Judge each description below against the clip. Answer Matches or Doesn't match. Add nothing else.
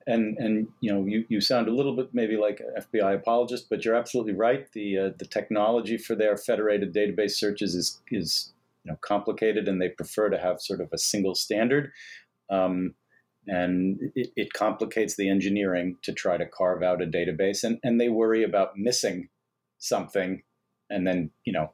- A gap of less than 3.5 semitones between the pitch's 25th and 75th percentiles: Matches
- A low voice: Matches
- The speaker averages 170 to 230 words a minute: Matches